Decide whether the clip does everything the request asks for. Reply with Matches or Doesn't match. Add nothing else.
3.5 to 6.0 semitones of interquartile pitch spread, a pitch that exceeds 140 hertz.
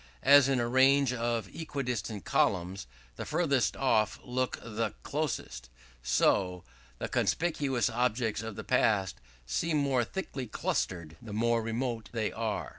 Doesn't match